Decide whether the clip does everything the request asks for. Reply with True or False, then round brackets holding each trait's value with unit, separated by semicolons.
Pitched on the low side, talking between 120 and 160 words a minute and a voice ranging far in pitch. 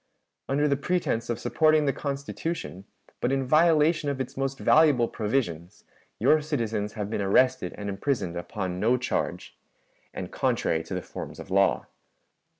True (130 Hz; 150 wpm; 6.1 semitones)